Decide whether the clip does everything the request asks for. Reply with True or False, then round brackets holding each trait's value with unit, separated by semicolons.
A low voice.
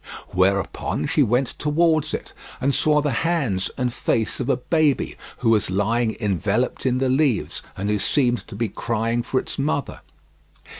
True (120 Hz)